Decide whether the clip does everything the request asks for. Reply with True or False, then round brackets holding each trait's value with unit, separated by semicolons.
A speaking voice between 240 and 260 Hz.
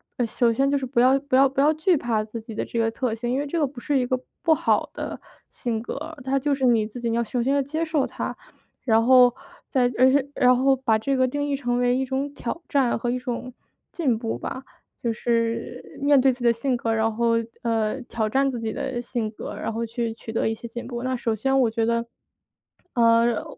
True (245 Hz)